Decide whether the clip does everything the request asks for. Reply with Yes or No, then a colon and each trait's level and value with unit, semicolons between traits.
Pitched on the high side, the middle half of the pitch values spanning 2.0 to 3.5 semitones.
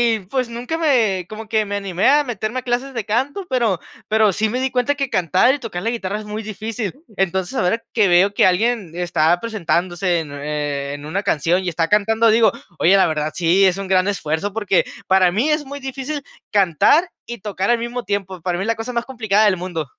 No: high, 205 Hz; average, 4.8 semitones